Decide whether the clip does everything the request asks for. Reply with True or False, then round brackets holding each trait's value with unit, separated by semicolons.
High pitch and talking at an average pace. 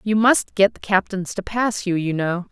False (195 Hz; 240 wpm)